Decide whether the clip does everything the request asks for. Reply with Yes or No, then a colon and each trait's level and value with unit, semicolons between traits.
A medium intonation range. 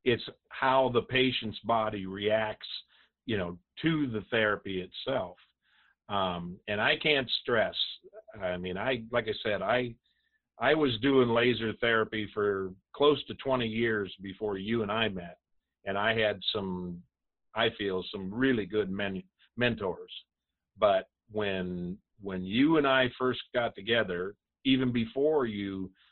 Yes: average, 4.4 semitones